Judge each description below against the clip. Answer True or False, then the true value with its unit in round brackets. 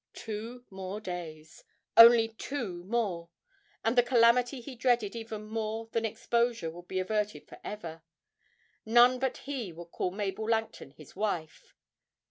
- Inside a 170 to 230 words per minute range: False (140 wpm)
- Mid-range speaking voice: False (220 Hz)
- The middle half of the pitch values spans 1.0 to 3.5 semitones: False (4.2 semitones)